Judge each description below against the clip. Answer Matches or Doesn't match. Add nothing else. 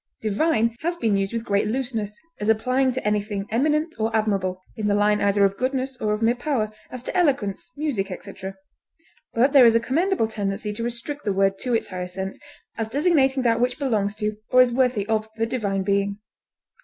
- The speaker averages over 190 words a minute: Matches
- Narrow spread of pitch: Doesn't match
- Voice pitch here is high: Matches